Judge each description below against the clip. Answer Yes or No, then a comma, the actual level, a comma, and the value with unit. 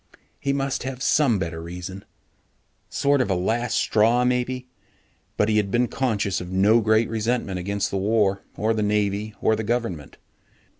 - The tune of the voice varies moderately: Yes, average, 3.8 semitones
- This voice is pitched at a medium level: No, low, 110 Hz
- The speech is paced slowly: No, average, 165 wpm